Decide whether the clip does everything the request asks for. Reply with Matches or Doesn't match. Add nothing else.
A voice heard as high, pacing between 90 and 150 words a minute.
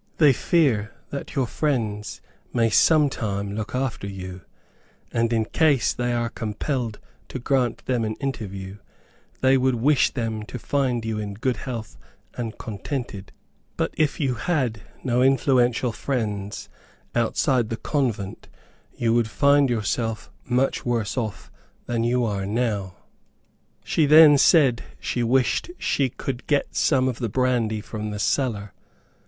Doesn't match